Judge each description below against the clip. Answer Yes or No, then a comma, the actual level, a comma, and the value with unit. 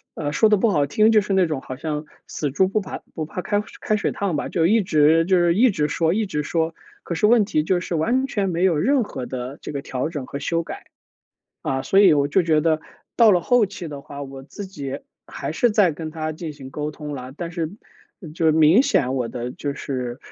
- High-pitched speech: No, medium, 160 Hz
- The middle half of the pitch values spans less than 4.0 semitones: No, average, 5.0 semitones